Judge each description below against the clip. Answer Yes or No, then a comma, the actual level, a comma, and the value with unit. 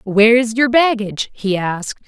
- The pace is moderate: Yes, average, 145 wpm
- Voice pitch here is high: Yes, high, 220 Hz